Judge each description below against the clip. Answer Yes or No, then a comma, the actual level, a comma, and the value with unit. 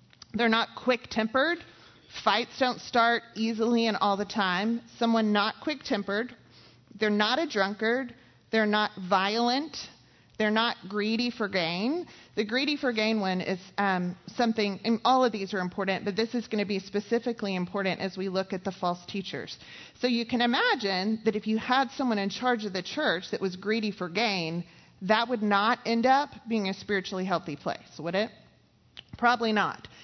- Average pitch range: Yes, average, 3.5 semitones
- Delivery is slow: No, average, 175 wpm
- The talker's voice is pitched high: Yes, high, 215 Hz